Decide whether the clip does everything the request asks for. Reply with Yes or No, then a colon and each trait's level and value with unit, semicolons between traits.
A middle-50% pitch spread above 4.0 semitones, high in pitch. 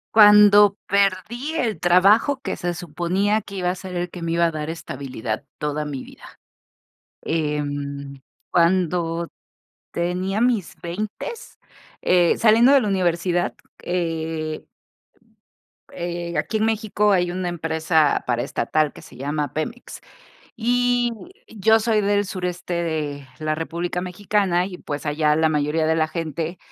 No: average, 4.4 semitones; medium, 175 Hz